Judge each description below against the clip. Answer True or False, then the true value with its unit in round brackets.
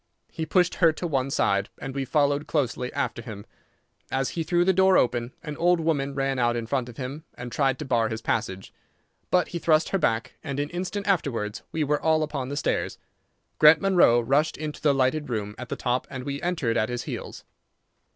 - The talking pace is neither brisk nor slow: False (210 wpm)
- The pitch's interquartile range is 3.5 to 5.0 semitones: True (4.6 semitones)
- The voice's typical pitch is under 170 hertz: True (140 Hz)